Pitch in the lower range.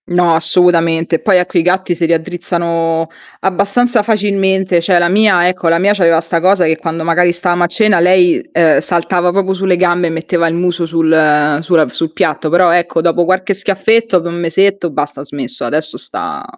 No: medium, 175 Hz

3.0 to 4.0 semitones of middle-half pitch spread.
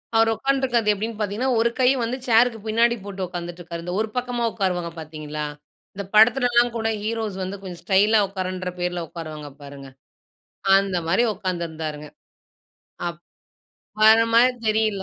No: average, 4.6 semitones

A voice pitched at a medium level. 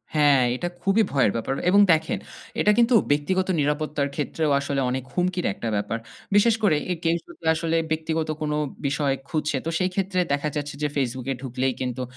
Yes: medium, 150 Hz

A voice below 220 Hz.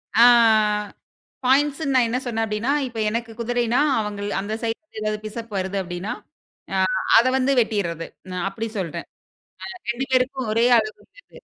No: high, 225 Hz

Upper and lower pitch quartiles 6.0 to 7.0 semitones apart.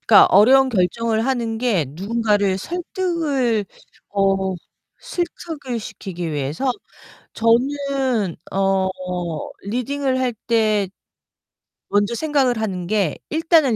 No: wide, 5.4 semitones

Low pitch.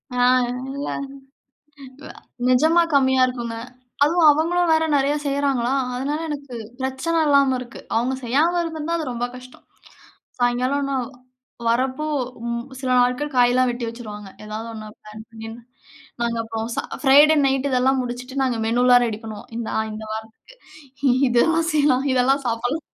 No: very high, 255 Hz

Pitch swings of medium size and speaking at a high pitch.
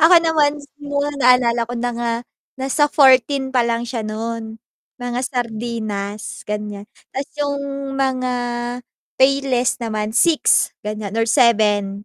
Yes: average, 3.6 semitones; high, 240 Hz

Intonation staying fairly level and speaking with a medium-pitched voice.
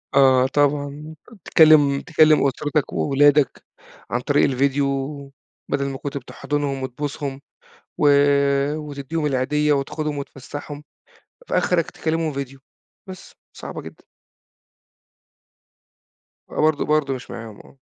Yes: narrow, 1.7 semitones; medium, 145 Hz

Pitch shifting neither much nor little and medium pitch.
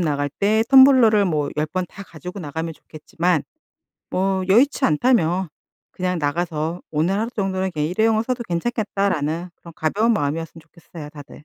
Yes: average, 4.6 semitones; medium, 180 Hz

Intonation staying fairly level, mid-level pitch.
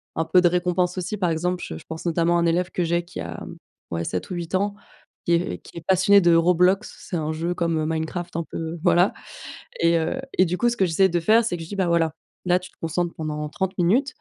Yes: narrow, 1.9 semitones; medium, 175 Hz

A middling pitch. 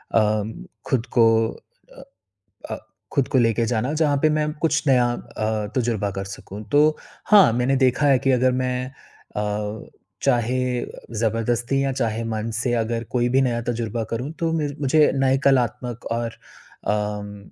No: low, 120 Hz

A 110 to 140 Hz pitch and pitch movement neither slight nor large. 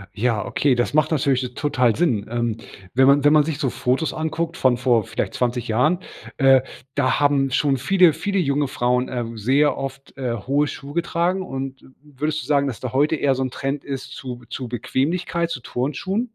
Yes: low, 135 Hz; average, 3.2 semitones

